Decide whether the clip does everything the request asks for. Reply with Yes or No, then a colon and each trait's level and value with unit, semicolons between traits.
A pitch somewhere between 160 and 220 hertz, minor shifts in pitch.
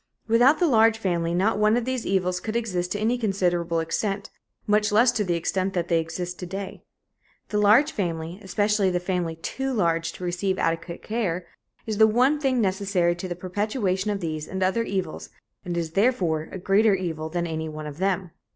No: high, 190 Hz; average, 3.8 semitones